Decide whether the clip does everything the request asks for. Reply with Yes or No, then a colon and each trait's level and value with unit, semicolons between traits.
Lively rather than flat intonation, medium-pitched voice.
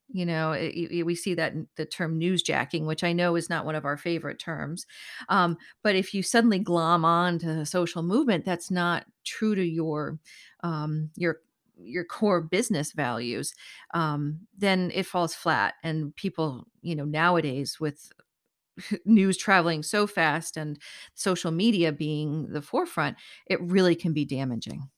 No: average, 2.9 semitones; medium, 170 Hz